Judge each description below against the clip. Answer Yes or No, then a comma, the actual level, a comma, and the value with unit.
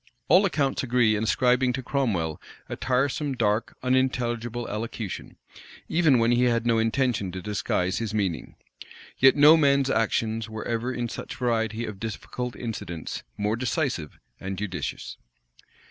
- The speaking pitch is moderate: No, low, 115 Hz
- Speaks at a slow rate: No, average, 145 wpm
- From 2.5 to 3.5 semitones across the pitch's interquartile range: Yes, average, 3.2 semitones